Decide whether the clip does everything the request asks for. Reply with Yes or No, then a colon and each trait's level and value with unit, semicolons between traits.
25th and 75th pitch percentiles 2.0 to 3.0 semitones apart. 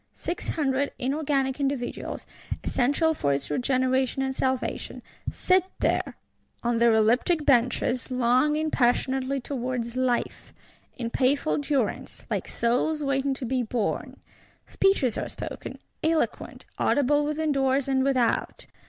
Yes: average, 2.7 semitones